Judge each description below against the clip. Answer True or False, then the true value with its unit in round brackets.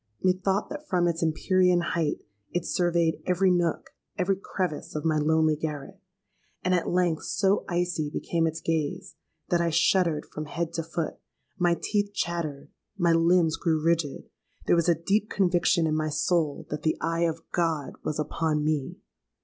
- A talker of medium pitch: True (170 Hz)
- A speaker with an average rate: True (160 wpm)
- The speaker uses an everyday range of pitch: False (2.2 semitones)